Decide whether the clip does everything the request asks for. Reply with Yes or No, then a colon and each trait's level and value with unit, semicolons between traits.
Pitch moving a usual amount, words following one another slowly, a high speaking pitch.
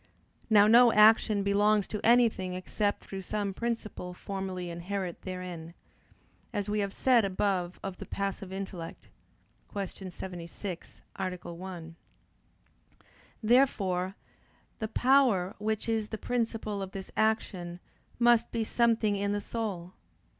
Yes: average, 3.0 semitones; slow, 125 wpm; high, 200 Hz